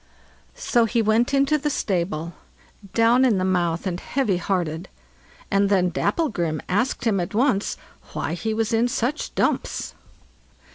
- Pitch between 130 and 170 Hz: No, high, 210 Hz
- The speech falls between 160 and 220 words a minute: No, average, 145 wpm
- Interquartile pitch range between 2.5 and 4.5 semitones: No, average, 5.3 semitones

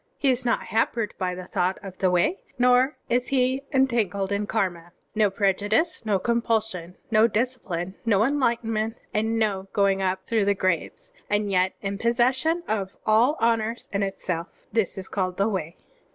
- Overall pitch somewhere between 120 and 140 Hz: No, high, 215 Hz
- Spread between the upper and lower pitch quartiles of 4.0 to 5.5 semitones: No, average, 3.6 semitones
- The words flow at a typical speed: Yes, average, 170 wpm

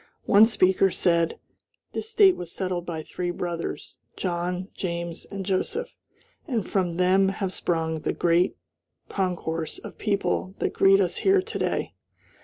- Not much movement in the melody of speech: Yes, narrow, 2.2 semitones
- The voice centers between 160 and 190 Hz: Yes, medium, 185 Hz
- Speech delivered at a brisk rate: No, average, 145 wpm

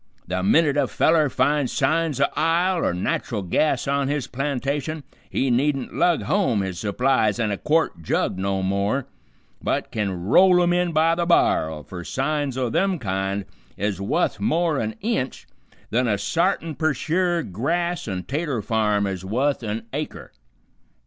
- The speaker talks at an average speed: Yes, average, 160 wpm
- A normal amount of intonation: No, wide, 7.8 semitones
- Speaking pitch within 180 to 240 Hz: No, low, 135 Hz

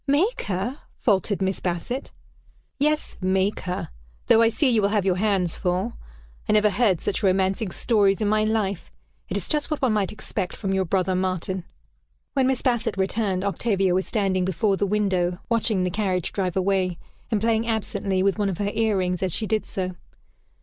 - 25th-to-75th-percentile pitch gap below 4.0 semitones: Yes, average, 2.8 semitones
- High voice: Yes, high, 200 Hz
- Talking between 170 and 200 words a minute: Yes, average, 190 wpm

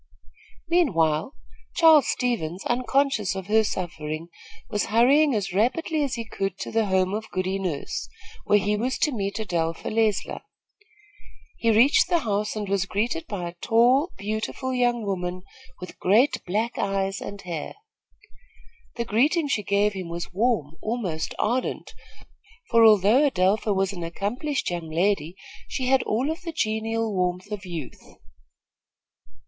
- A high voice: Yes, high, 210 Hz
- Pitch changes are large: No, average, 4.7 semitones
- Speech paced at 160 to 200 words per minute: No, average, 145 wpm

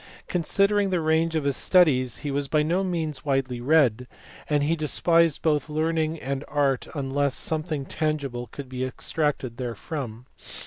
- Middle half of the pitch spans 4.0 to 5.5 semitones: No, average, 3.3 semitones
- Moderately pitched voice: Yes, medium, 150 Hz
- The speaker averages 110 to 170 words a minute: Yes, average, 155 wpm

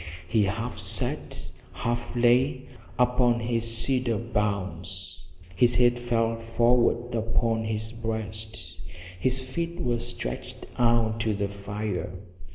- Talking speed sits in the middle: No, slow, 115 wpm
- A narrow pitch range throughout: Yes, narrow, 2.0 semitones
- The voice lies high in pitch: No, low, 115 Hz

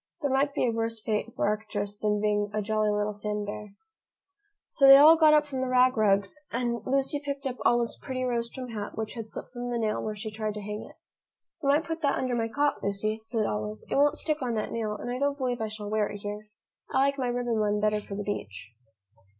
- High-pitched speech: Yes, high, 225 Hz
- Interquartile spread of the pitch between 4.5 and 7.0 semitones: No, average, 3.7 semitones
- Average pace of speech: No, fast, 245 wpm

